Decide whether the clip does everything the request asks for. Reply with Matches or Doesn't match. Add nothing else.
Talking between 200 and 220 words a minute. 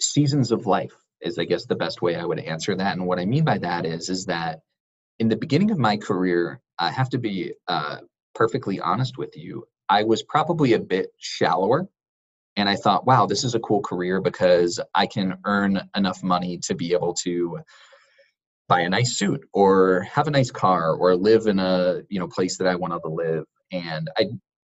Matches